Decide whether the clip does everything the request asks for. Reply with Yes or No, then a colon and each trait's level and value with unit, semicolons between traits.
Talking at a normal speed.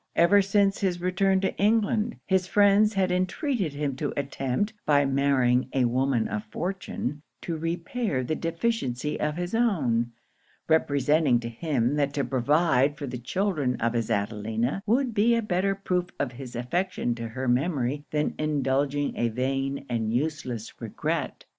Yes: average, 155 wpm